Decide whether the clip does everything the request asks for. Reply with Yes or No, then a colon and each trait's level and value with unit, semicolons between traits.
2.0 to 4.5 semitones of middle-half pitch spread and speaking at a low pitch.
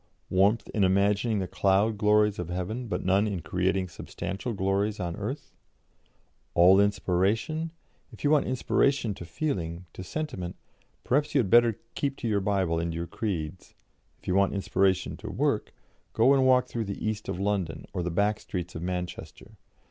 Yes: average, 3.5 semitones; low, 100 Hz